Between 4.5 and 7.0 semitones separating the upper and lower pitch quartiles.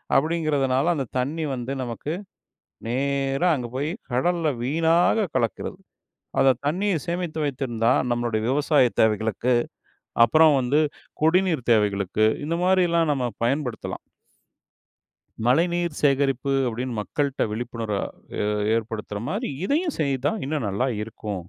Yes: average, 5.1 semitones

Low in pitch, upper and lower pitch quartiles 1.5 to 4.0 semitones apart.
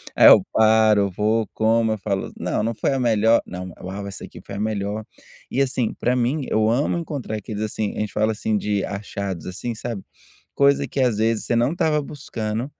Yes: low, 110 Hz; average, 2.7 semitones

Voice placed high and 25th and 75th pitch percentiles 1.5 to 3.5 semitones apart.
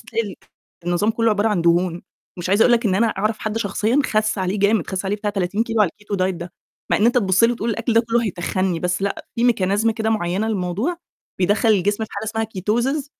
Yes: high, 210 Hz; average, 3.1 semitones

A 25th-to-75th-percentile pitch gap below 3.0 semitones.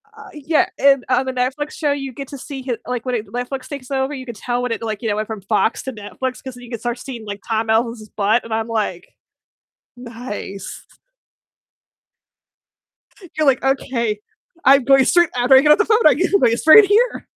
No: average, 3.4 semitones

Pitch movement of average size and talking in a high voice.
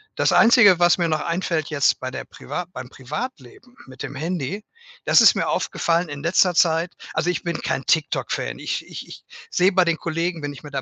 No: average, 3.6 semitones; medium, 165 Hz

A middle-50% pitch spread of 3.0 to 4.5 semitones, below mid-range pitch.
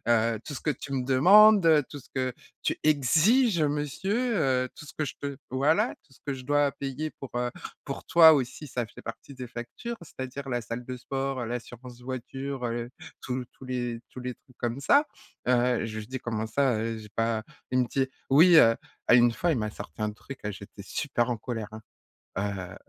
Yes: average, 3.5 semitones; low, 130 Hz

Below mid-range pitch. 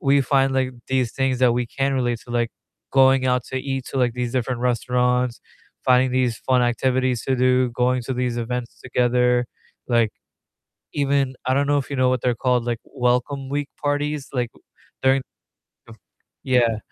Yes: low, 125 Hz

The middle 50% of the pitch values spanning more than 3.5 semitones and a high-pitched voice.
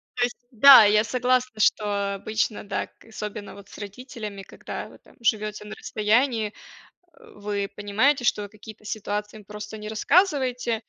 No: average, 2.8 semitones; high, 215 Hz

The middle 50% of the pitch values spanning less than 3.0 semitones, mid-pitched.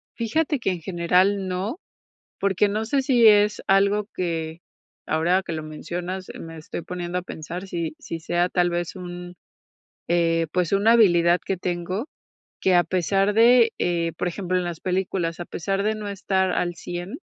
Yes: narrow, 2.5 semitones; medium, 180 Hz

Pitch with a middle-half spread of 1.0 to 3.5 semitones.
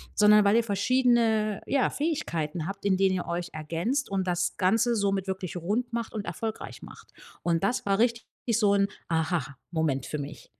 No: average, 4.5 semitones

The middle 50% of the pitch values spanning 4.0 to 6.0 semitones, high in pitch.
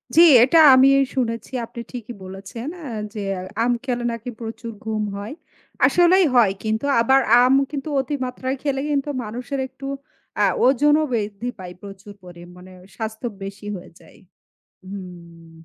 Yes: average, 4.6 semitones; high, 230 Hz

